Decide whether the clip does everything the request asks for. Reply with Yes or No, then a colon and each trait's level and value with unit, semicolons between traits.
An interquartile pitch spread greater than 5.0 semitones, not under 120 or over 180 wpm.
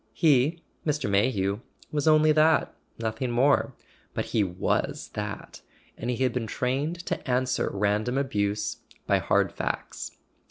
Yes: wide, 5.4 semitones; average, 145 wpm